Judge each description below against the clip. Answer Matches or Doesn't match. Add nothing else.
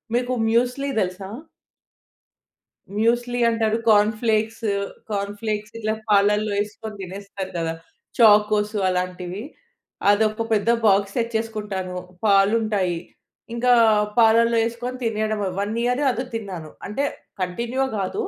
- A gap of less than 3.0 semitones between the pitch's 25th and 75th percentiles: Matches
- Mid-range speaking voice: Doesn't match